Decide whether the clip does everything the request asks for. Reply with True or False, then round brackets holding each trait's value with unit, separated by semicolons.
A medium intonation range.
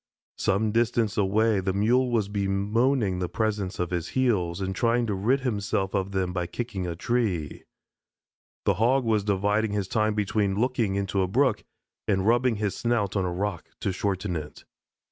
True (3.2 semitones)